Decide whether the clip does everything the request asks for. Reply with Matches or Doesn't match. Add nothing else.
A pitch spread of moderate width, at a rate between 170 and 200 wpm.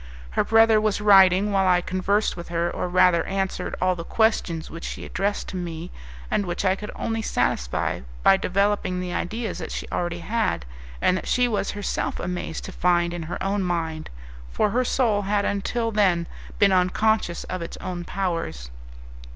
Matches